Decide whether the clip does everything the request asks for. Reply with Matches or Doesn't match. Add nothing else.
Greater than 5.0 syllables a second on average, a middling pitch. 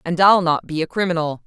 Matches